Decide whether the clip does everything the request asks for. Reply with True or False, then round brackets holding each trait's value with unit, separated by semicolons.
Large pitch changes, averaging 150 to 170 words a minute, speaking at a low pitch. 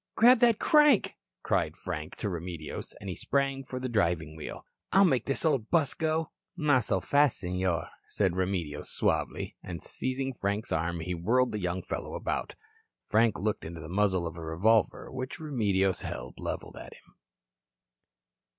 True (7.5 semitones; 165 wpm; 105 Hz)